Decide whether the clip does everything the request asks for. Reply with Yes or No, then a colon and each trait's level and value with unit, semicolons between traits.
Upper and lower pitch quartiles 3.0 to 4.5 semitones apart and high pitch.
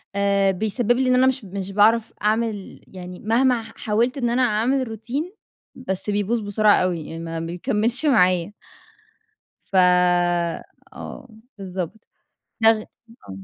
Yes: average, 3.8 semitones; high, 215 Hz